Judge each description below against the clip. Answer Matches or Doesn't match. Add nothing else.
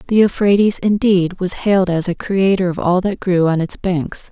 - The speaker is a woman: Matches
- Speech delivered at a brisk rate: Matches